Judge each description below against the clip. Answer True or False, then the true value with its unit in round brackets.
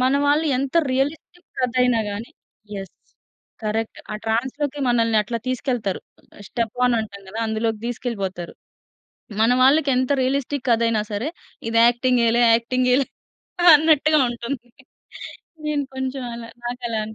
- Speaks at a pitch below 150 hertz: False (245 Hz)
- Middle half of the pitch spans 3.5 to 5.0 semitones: False (3.0 semitones)